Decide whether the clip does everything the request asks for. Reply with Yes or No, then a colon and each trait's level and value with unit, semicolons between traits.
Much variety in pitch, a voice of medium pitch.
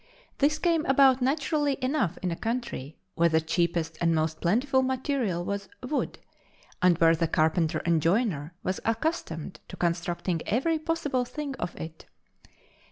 No: wide, 8.3 semitones; high, 195 Hz